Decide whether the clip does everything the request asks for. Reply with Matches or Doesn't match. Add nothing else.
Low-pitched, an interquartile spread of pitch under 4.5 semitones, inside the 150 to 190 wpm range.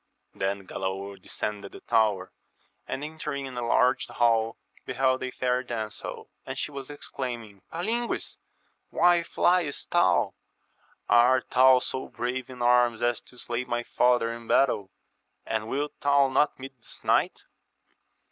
Doesn't match